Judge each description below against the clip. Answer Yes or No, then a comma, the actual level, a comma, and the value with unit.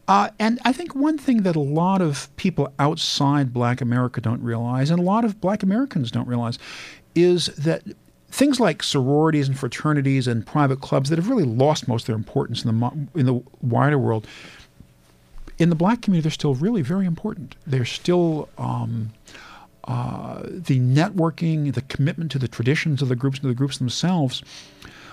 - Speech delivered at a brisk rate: No, average, 180 wpm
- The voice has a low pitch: No, medium, 145 Hz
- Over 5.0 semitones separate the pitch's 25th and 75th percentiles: Yes, wide, 5.6 semitones